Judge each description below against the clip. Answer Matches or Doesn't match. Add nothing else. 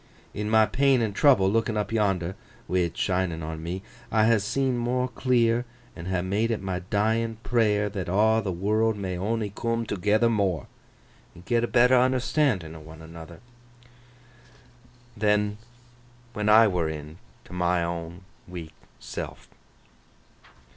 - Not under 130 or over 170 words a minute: Matches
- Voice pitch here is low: Matches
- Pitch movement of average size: Matches